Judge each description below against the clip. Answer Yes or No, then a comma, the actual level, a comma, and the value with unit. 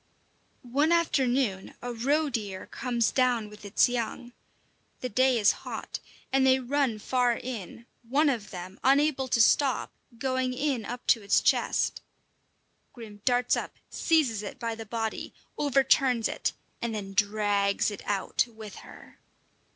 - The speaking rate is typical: Yes, average, 145 wpm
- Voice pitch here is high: Yes, high, 240 Hz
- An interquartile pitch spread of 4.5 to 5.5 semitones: No, average, 3.7 semitones